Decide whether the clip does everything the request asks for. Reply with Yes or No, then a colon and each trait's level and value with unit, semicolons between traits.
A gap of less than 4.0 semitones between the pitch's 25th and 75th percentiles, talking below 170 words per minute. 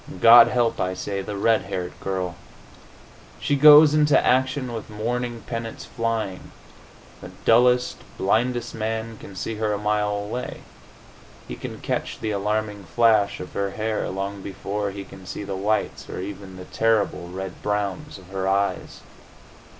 Yes: average, 2.8 semitones; average, 155 wpm